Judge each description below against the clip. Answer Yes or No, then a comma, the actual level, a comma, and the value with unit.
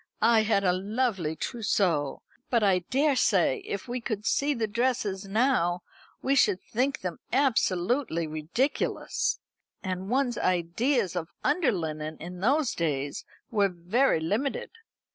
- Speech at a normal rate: No, slow, 130 wpm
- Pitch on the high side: Yes, high, 200 Hz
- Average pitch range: No, wide, 6.2 semitones